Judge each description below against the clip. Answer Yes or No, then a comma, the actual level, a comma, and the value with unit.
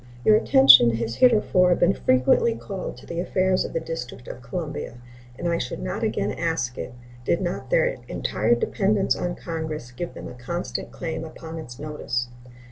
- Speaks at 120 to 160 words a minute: No, average, 175 wpm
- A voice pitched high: No, medium, 165 Hz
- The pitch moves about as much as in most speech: No, wide, 6.6 semitones